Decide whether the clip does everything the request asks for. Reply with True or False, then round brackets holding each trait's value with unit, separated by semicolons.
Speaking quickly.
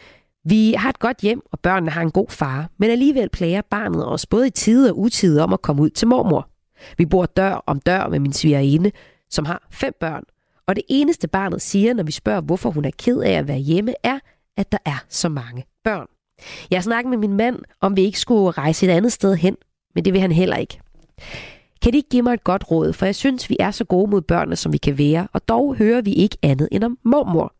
True (245 wpm)